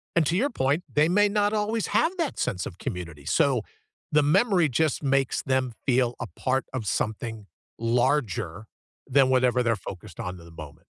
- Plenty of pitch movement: Yes, wide, 6.6 semitones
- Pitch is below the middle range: Yes, low, 130 Hz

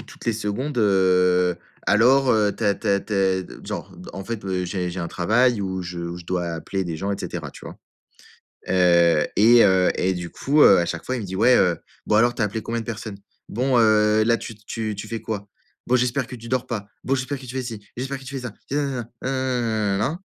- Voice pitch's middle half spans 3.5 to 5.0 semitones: Yes, average, 4.5 semitones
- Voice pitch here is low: Yes, low, 105 Hz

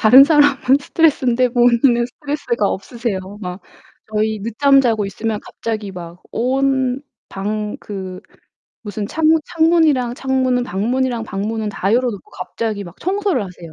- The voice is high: Yes, high, 235 Hz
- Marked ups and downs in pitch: No, average, 4.4 semitones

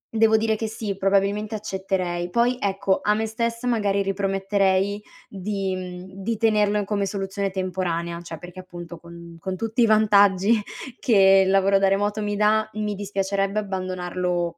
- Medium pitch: No, high, 195 Hz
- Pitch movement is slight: Yes, narrow, 2.2 semitones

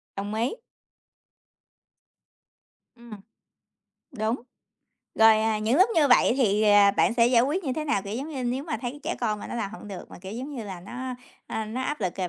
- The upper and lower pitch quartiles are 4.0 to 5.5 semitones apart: No, average, 3.6 semitones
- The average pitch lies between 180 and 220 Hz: No, high, 235 Hz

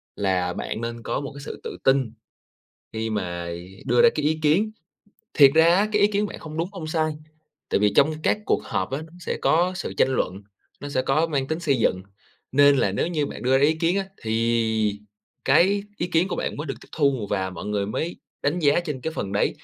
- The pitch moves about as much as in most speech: No, wide, 6.5 semitones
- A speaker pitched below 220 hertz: Yes, medium, 140 Hz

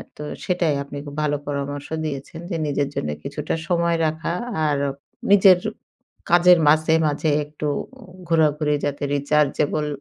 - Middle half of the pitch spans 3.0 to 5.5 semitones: No, narrow, 2.4 semitones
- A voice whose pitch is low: No, medium, 150 Hz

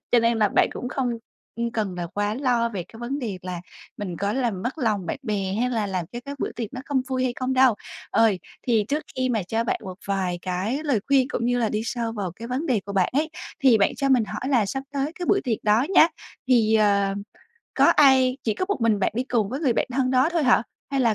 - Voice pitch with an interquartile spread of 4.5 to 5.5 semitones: No, average, 4.1 semitones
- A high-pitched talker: Yes, high, 235 Hz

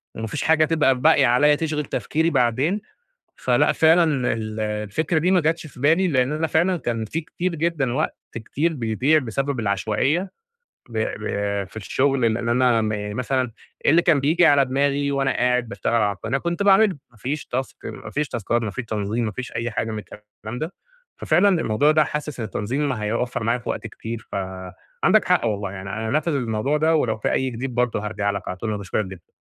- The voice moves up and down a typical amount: No, wide, 5.7 semitones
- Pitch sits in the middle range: No, low, 125 Hz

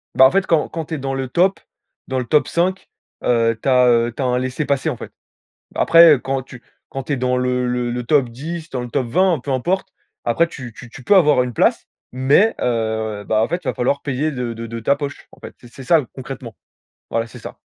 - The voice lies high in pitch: No, low, 130 Hz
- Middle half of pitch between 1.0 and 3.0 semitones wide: No, average, 3.6 semitones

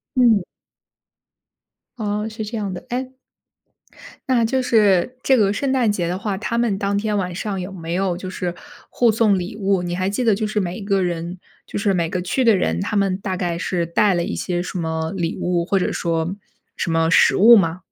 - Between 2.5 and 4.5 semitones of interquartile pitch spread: Yes, average, 3.5 semitones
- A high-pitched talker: Yes, high, 195 Hz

